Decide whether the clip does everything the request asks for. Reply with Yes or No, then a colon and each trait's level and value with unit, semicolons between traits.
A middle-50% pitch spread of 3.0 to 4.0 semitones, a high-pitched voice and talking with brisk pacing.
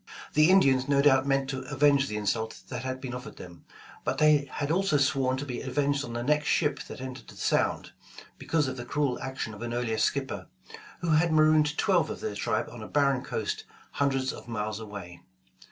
No: average, 3.3 semitones; low, 135 Hz; fast, 215 wpm